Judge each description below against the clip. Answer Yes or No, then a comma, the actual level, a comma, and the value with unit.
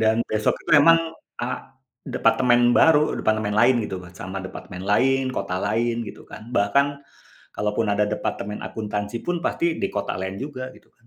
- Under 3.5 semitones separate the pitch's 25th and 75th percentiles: No, average, 3.9 semitones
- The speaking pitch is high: No, low, 110 Hz